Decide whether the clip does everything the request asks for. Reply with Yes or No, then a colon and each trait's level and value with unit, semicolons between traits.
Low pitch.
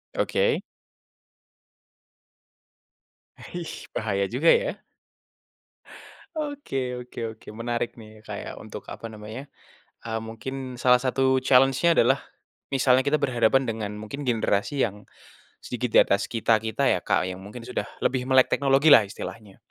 Yes: low, 125 Hz